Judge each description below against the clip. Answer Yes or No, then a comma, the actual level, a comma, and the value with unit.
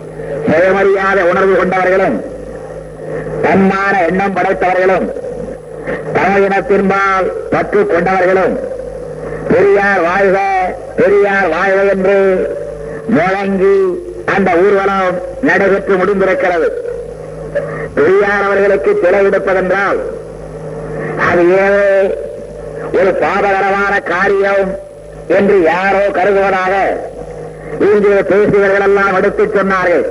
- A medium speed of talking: No, slow, 70 wpm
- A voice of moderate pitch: No, high, 195 Hz